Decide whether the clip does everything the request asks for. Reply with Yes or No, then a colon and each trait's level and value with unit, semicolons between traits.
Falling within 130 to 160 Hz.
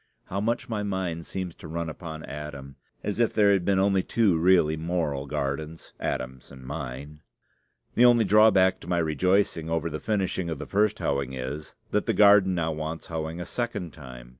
No: very low, 85 Hz